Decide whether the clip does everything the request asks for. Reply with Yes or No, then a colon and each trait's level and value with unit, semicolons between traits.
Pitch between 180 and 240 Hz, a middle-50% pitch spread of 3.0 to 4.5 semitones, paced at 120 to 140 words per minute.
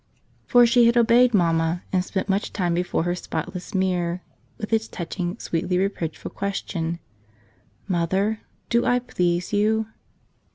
Yes: medium, 185 Hz; average, 4.1 semitones; slow, 135 wpm